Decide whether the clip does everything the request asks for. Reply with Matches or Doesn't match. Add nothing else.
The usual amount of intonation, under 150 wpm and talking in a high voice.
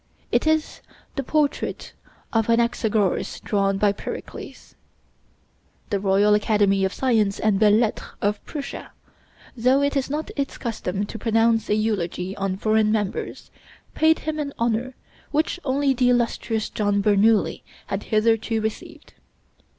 Matches